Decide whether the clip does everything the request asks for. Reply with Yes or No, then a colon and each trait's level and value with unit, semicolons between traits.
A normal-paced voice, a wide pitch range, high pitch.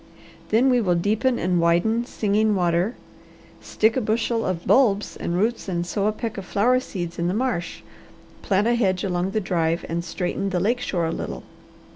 No: average, 190 wpm; average, 4.3 semitones; high, 200 Hz